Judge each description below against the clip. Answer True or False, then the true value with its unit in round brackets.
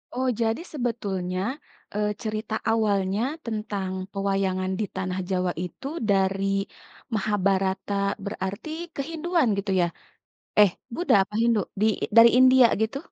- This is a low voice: False (205 Hz)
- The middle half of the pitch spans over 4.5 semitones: False (3.2 semitones)